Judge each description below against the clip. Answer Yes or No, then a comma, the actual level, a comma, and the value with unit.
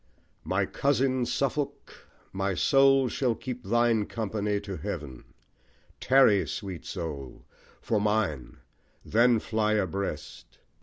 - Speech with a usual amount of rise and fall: Yes, average, 4.5 semitones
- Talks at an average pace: No, slow, 105 wpm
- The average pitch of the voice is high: No, low, 110 Hz